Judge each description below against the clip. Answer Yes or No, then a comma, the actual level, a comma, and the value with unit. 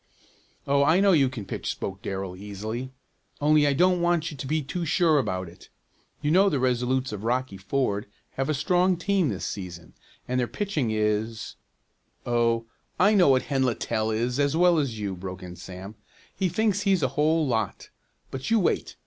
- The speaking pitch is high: No, low, 130 Hz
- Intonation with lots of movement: Yes, wide, 7.0 semitones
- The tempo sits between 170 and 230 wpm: Yes, average, 190 wpm